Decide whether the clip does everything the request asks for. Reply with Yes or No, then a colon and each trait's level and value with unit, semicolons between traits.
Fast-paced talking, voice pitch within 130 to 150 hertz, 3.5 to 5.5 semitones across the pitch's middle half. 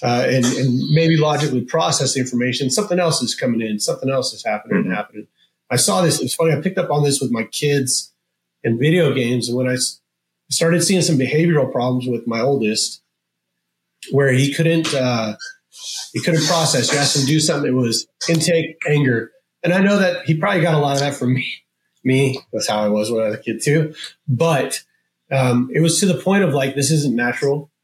Yes: fast, 215 wpm; medium, 140 Hz; average, 4.7 semitones